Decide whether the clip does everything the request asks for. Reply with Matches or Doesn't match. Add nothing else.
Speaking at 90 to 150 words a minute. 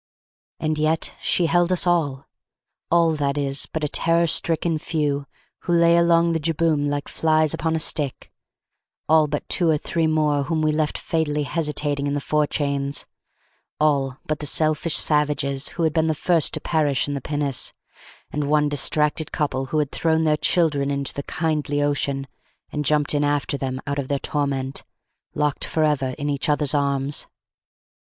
Doesn't match